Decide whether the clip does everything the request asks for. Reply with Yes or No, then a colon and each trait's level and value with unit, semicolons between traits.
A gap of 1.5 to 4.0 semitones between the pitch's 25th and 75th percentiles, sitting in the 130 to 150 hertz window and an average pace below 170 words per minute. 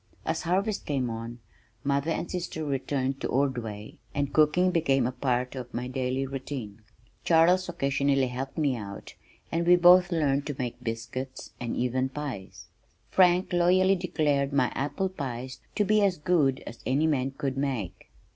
No: average, 4.8 semitones; medium, 140 Hz; average, 155 wpm